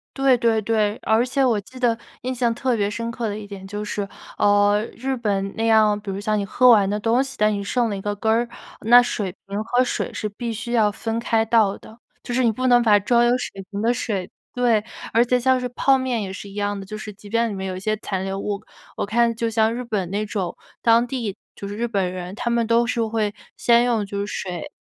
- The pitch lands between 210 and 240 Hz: Yes, high, 220 Hz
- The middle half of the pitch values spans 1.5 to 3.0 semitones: Yes, average, 2.7 semitones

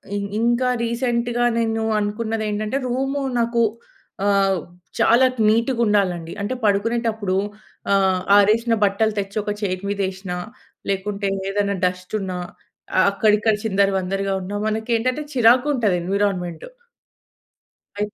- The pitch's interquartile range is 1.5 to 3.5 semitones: Yes, average, 2.9 semitones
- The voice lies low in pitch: No, high, 210 Hz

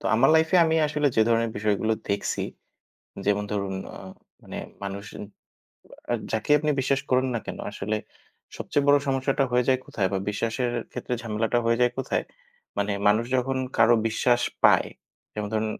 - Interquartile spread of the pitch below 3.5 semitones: No, average, 3.9 semitones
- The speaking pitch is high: No, low, 115 Hz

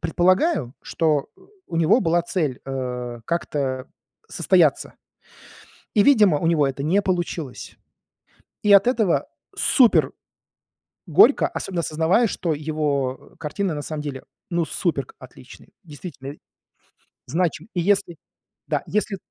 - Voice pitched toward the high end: No, medium, 165 Hz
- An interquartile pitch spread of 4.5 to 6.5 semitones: Yes, average, 4.8 semitones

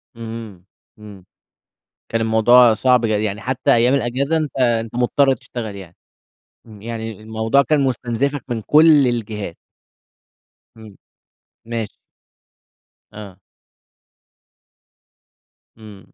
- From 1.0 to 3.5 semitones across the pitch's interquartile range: Yes, average, 2.9 semitones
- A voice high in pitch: No, low, 115 Hz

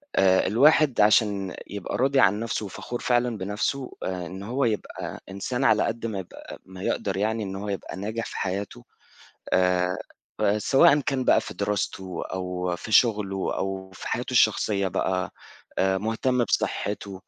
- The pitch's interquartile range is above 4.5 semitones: No, average, 3.4 semitones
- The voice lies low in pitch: Yes, low, 100 Hz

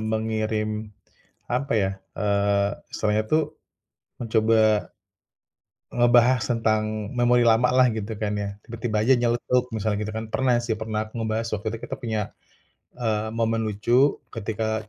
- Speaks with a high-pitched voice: No, low, 110 Hz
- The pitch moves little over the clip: Yes, narrow, 1.8 semitones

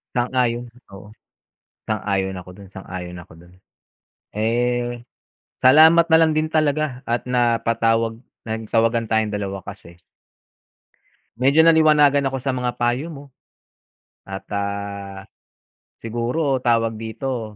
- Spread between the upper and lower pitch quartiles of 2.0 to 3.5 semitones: No, average, 4.4 semitones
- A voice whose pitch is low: Yes, low, 115 Hz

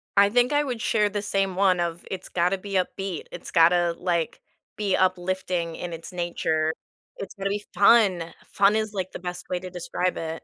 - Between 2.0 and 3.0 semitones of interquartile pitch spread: Yes, narrow, 2.5 semitones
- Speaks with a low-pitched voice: No, medium, 185 Hz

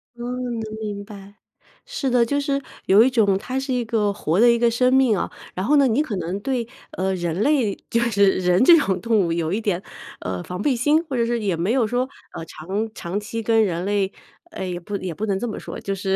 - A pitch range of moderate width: Yes, average, 4.3 semitones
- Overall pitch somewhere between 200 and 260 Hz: Yes, high, 215 Hz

